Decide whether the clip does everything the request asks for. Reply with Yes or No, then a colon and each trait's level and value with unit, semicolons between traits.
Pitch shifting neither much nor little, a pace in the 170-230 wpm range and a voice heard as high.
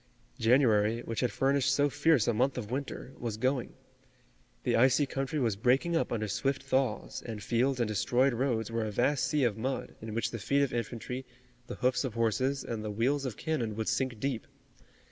No: average, 3.2 semitones; average, 200 wpm; low, 125 Hz